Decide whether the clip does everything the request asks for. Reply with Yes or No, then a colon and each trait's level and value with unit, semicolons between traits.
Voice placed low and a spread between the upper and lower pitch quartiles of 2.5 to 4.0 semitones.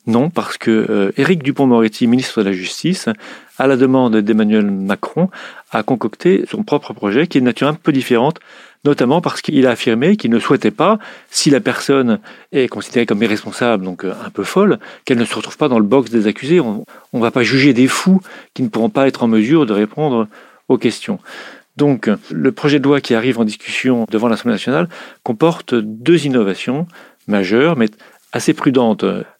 No: low, 125 Hz; average, 4.5 semitones